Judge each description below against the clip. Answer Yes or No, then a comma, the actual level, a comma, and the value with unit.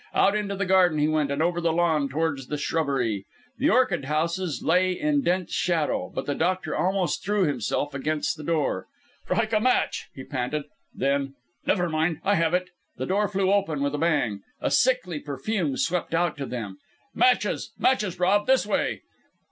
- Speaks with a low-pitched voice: No, medium, 165 Hz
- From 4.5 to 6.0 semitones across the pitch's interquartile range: Yes, average, 4.8 semitones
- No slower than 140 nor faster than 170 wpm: No, average, 180 wpm